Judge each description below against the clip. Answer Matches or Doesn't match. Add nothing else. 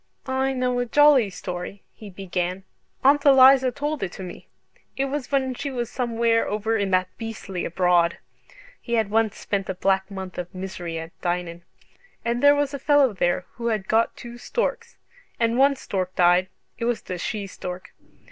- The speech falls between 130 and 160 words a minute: Doesn't match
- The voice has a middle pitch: Doesn't match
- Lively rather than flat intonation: Matches